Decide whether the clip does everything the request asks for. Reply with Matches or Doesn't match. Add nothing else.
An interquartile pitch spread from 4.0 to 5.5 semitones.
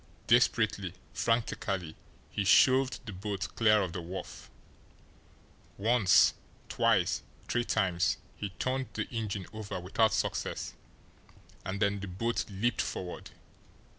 Doesn't match